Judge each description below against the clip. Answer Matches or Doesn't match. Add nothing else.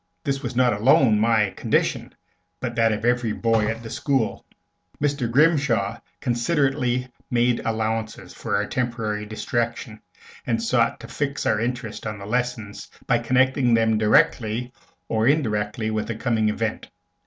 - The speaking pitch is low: Matches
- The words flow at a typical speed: Matches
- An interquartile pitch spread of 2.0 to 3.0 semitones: Matches